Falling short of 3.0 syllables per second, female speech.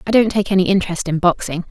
No: 7.1 syllables/s; female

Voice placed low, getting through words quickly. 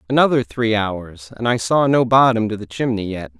Yes: low, 115 Hz; fast, 210 wpm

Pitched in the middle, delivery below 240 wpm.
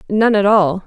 No: high, 200 Hz; fast, 210 wpm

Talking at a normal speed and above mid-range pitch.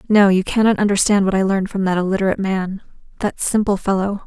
Yes: average, 185 wpm; high, 195 Hz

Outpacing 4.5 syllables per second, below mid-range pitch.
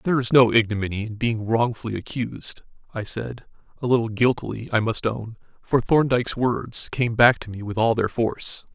Yes: 5.3 syllables/s; low, 115 Hz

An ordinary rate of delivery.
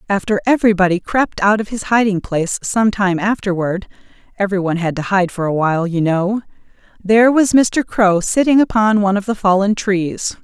Yes: average, 180 wpm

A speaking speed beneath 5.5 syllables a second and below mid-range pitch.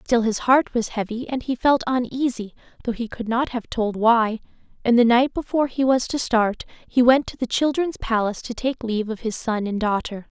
No: 5.3 syllables/s; high, 235 Hz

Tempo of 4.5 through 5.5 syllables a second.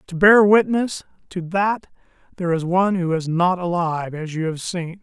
Yes: 5.0 syllables/s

